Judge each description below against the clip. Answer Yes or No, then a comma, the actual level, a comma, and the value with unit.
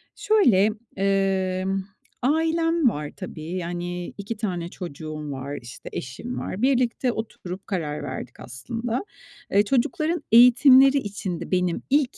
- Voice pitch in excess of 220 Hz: No, high, 195 Hz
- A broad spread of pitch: Yes, wide, 6.4 semitones